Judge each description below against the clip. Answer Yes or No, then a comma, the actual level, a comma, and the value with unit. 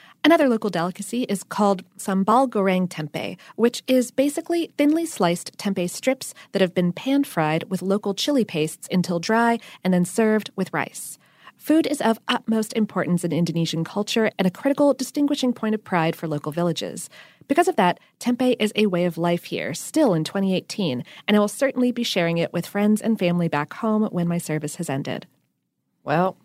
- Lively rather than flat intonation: Yes, wide, 5.8 semitones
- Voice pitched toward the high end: Yes, high, 200 Hz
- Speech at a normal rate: Yes, average, 180 wpm